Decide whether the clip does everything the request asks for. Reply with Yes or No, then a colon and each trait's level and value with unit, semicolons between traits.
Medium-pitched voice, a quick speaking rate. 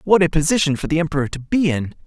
Yes: medium, 160 Hz; fast, 260 wpm